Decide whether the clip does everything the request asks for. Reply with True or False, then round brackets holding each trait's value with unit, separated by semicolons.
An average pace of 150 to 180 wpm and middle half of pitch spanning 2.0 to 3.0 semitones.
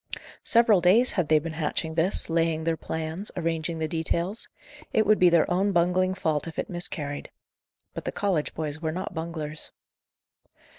True (165 wpm; 2.6 semitones)